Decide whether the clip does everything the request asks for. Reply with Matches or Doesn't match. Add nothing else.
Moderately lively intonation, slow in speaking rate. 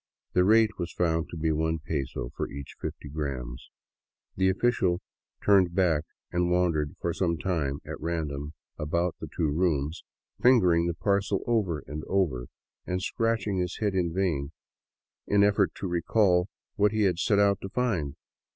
Doesn't match